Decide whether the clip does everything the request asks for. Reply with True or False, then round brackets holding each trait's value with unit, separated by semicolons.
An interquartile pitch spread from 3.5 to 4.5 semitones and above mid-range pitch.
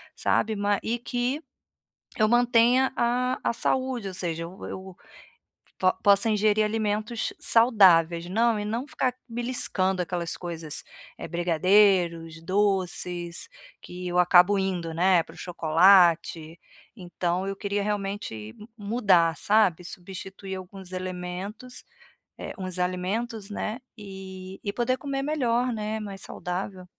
True (3.8 semitones; 195 Hz)